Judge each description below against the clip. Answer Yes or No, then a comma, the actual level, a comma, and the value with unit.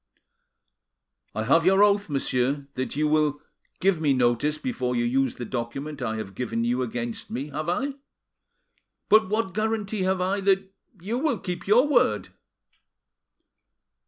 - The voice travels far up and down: Yes, wide, 7.9 semitones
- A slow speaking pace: No, average, 150 wpm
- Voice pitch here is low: No, medium, 155 Hz